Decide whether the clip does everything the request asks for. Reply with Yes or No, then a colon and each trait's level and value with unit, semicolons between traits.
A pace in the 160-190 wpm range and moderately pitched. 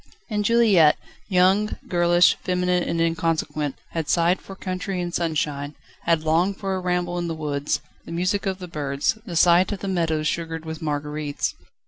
Yes: average, 170 wpm; medium, 170 Hz